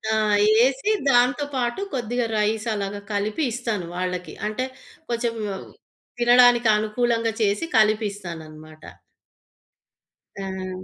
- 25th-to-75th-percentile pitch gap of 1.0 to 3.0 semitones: No, average, 3.7 semitones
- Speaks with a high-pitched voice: Yes, high, 220 Hz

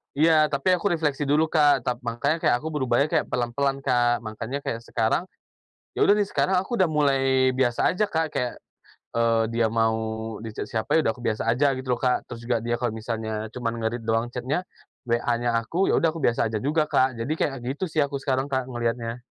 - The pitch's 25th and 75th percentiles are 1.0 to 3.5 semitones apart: No, average, 4.1 semitones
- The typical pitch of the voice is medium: No, low, 125 Hz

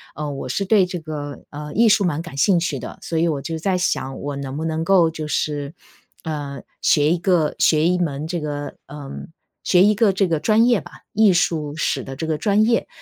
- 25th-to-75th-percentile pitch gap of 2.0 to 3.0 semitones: No, average, 3.8 semitones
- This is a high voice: No, medium, 160 Hz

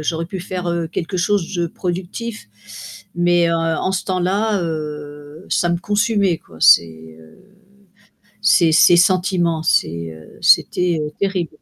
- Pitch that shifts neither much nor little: Yes, average, 3.2 semitones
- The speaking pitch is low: No, medium, 175 Hz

